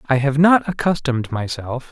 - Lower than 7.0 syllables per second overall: Yes, 5.0 syllables/s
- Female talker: No, male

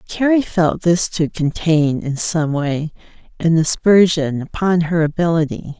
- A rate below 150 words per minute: Yes, slow, 135 wpm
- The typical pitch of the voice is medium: Yes, medium, 165 Hz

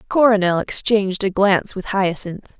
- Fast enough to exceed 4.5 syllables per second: Yes, 5.0 syllables/s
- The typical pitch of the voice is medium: No, high, 195 Hz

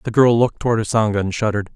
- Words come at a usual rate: No, fast, 240 wpm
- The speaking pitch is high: No, low, 110 Hz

